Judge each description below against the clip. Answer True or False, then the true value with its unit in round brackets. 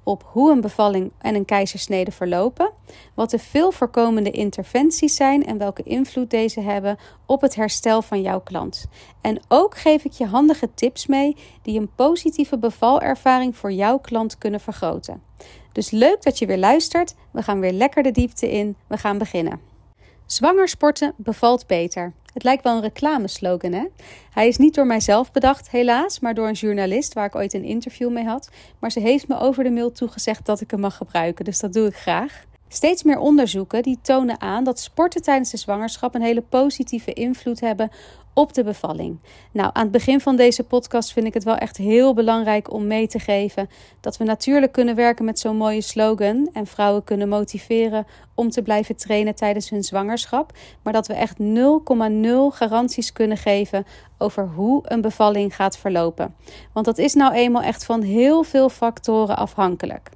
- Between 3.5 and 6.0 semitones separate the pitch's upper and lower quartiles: True (3.8 semitones)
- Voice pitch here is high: True (225 Hz)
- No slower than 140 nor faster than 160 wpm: False (185 wpm)